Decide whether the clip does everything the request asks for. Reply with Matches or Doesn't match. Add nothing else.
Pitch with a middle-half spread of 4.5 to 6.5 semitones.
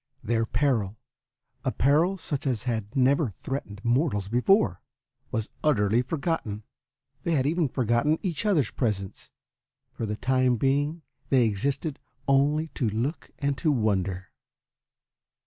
Matches